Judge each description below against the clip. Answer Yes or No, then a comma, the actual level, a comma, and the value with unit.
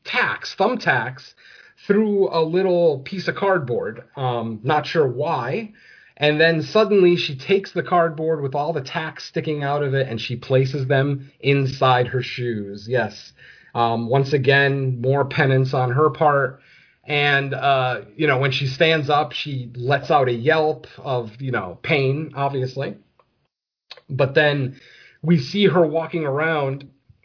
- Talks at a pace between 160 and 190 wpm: No, average, 150 wpm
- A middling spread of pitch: Yes, average, 3.6 semitones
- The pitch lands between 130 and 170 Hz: Yes, medium, 140 Hz